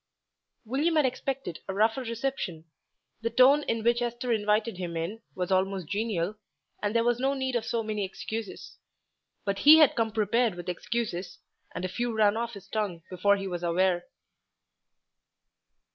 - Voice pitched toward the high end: Yes, high, 215 Hz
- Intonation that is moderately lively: Yes, average, 4.1 semitones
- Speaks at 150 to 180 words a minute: Yes, average, 165 wpm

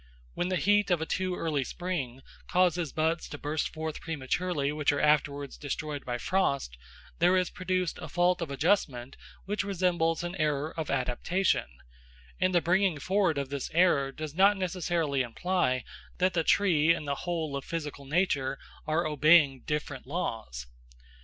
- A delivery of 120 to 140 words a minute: No, average, 160 wpm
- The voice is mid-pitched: Yes, medium, 160 Hz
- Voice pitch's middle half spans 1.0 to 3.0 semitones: No, average, 4.1 semitones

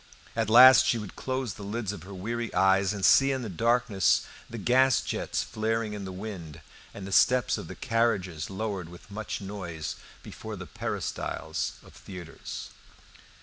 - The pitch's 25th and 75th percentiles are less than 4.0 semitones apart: Yes, average, 3.6 semitones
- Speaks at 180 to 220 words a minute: No, average, 165 wpm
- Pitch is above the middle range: No, low, 105 Hz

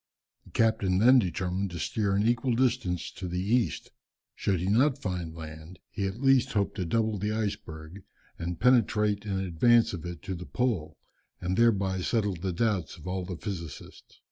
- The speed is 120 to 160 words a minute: No, average, 180 wpm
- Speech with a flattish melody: No, average, 4.0 semitones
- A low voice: Yes, low, 100 Hz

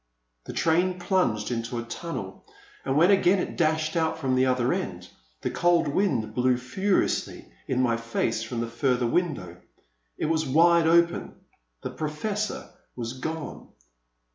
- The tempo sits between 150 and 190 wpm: Yes, average, 155 wpm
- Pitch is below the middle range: No, medium, 145 Hz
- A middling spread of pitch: No, wide, 6.4 semitones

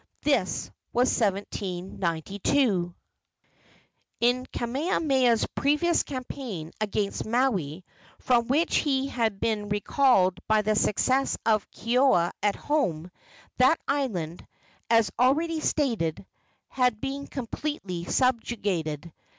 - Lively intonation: Yes, wide, 5.8 semitones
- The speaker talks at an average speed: No, slow, 100 wpm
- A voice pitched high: Yes, high, 230 Hz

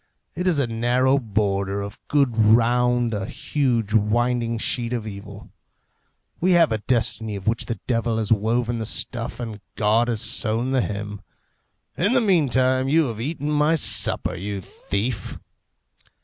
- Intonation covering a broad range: No, average, 3.4 semitones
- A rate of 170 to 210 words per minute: No, average, 155 wpm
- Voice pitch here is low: Yes, low, 115 Hz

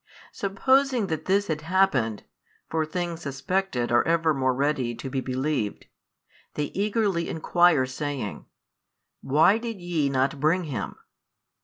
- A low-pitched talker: No, medium, 155 Hz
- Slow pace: Yes, slow, 125 wpm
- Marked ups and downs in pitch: Yes, wide, 5.9 semitones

